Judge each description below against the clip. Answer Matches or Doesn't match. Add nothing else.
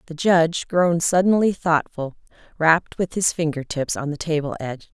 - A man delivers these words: Doesn't match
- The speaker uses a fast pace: Doesn't match